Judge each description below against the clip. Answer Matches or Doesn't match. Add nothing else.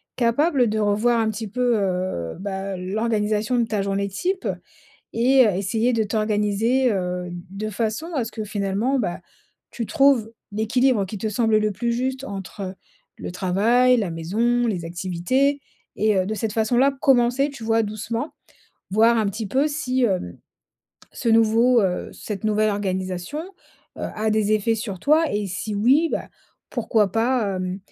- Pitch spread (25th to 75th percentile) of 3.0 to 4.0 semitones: Matches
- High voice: Matches